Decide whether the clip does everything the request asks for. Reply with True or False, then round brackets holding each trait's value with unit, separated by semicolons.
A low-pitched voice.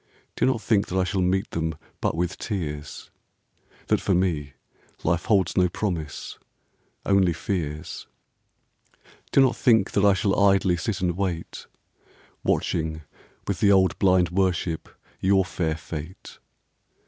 True (90 Hz)